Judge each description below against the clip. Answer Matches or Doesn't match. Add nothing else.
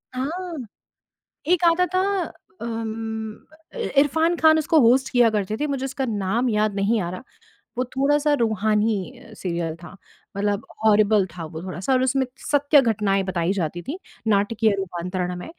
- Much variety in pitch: Matches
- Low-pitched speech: Doesn't match